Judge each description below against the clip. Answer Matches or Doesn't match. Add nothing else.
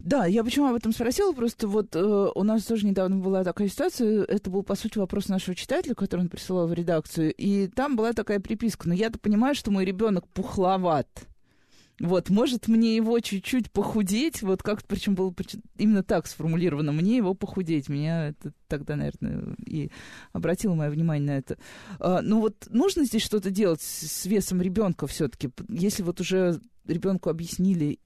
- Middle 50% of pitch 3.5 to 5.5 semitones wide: Matches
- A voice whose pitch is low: Doesn't match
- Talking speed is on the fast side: Matches